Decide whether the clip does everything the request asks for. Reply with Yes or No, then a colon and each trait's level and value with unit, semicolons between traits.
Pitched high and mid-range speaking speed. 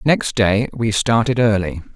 No: low, 110 Hz; average, 155 wpm